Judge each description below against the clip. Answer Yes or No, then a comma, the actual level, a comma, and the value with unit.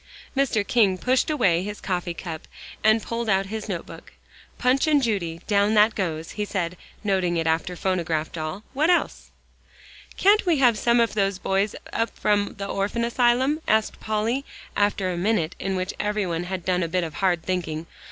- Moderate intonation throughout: Yes, average, 4.2 semitones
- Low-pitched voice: No, high, 200 Hz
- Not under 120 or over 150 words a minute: No, average, 180 wpm